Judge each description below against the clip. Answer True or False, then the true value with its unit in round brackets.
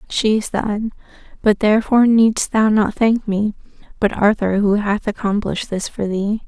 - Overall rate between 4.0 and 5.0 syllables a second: True (4.9 syllables/s)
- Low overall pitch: False (210 Hz)